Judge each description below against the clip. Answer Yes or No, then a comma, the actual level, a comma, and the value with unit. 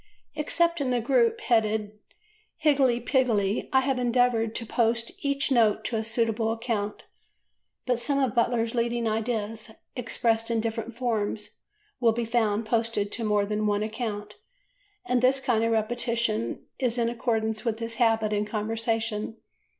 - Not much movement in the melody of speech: Yes, narrow, 1.9 semitones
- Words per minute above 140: Yes, average, 150 wpm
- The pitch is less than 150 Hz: No, high, 230 Hz